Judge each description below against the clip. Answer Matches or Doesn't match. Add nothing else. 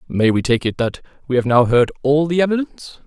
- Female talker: Doesn't match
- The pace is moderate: Doesn't match